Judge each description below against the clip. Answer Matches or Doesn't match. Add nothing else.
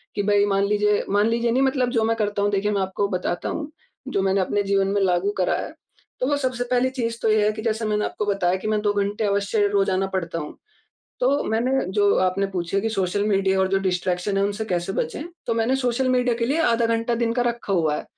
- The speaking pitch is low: Doesn't match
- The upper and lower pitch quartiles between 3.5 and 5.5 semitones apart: Doesn't match